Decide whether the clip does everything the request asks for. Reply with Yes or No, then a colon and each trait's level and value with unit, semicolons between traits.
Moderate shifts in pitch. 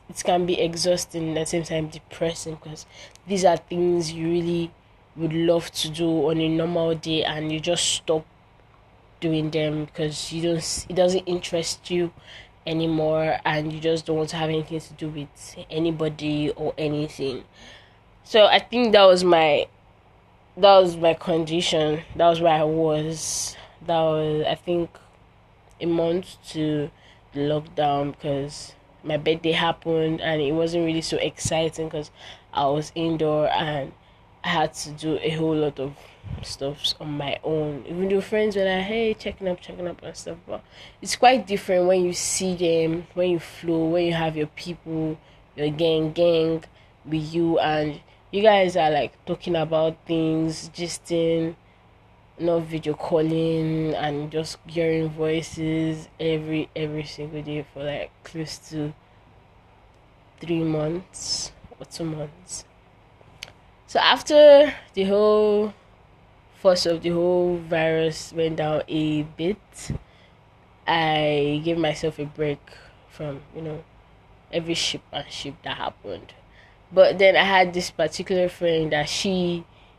No: narrow, 2.3 semitones